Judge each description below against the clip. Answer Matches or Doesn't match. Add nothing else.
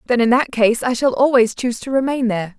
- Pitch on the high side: Matches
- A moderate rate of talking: Doesn't match